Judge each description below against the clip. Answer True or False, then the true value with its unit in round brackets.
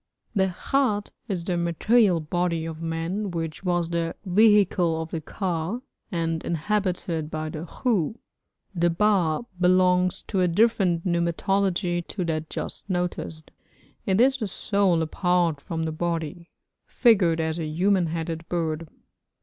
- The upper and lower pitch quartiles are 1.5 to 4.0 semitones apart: True (2.9 semitones)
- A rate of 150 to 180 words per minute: False (140 wpm)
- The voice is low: False (175 Hz)